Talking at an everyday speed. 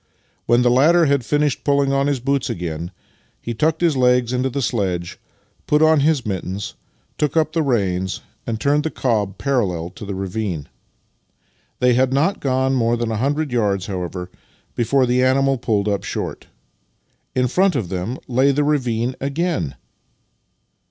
Yes: average, 165 wpm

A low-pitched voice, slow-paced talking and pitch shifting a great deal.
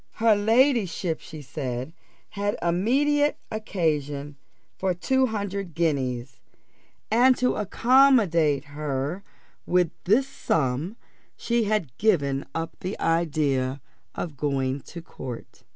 No: medium, 170 Hz; slow, 105 wpm; wide, 7.2 semitones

